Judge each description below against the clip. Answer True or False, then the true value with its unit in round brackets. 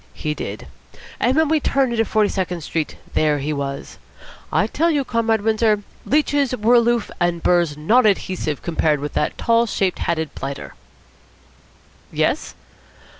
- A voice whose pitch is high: True (205 Hz)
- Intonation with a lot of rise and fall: True (7.2 semitones)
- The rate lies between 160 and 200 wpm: False (150 wpm)